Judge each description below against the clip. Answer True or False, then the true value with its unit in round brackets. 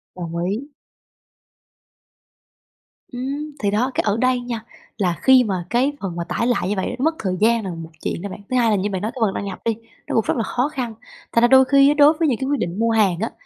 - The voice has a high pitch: True (230 Hz)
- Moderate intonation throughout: True (4.6 semitones)